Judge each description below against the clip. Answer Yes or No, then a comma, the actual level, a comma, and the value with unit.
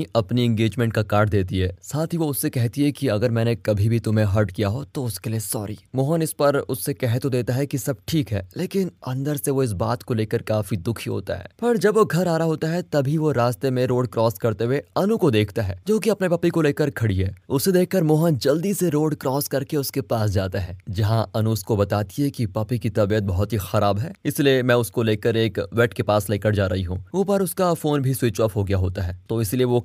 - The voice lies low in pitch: Yes, low, 120 Hz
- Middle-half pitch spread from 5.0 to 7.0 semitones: Yes, average, 5.3 semitones